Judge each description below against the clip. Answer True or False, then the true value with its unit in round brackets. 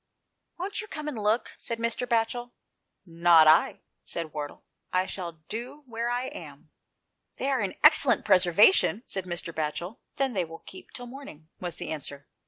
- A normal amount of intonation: False (6.6 semitones)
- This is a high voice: True (210 Hz)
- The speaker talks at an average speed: True (180 wpm)